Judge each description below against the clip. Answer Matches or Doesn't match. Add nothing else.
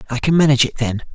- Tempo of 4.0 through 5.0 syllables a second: Doesn't match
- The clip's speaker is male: Matches